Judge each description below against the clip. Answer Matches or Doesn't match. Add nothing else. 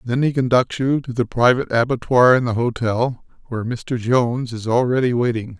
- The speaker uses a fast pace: Doesn't match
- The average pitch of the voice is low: Matches